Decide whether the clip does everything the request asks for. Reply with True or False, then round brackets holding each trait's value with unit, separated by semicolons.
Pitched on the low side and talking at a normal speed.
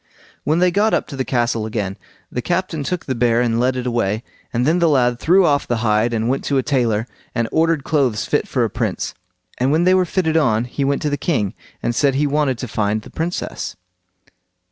False (130 Hz; 230 wpm)